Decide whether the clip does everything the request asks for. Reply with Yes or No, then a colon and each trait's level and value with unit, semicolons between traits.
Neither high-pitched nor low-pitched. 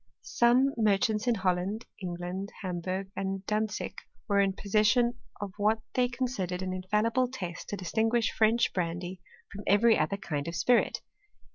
No: high, 200 Hz